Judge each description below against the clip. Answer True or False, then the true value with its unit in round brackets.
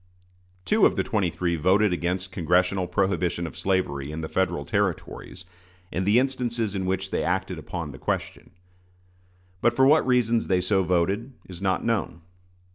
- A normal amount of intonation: True (3.0 semitones)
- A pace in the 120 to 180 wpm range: True (165 wpm)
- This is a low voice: True (95 Hz)